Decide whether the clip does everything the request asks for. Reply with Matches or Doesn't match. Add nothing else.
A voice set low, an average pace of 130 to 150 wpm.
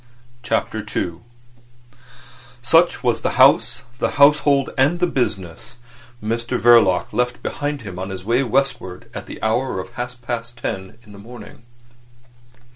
Matches